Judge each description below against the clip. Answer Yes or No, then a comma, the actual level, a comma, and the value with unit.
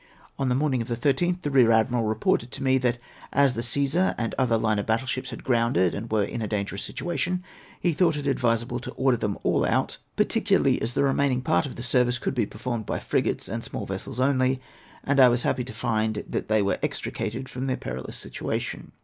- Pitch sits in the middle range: No, low, 125 Hz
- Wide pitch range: No, average, 3.1 semitones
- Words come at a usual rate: No, fast, 225 wpm